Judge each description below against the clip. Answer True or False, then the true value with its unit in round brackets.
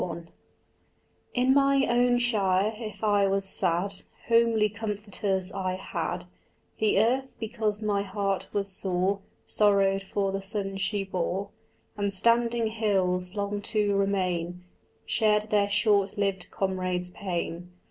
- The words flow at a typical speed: False (125 wpm)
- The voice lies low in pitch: False (200 Hz)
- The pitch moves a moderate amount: False (2.2 semitones)